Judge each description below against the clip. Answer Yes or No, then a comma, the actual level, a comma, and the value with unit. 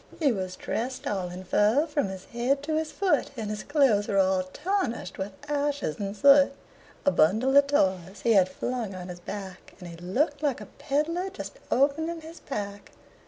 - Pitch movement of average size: No, wide, 7.2 semitones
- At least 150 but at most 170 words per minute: No, average, 190 wpm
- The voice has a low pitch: No, high, 235 Hz